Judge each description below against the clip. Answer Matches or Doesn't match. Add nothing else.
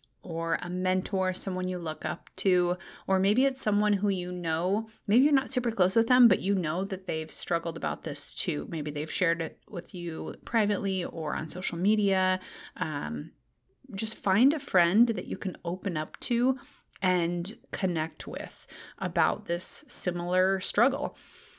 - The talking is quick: Doesn't match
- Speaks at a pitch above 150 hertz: Matches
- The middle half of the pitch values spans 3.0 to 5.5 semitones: Matches